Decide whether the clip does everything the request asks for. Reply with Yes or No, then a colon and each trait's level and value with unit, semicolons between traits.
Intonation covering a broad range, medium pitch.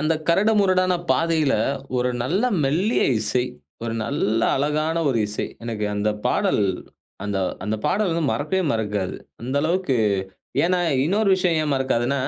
Yes: wide, 7.4 semitones; medium, 150 Hz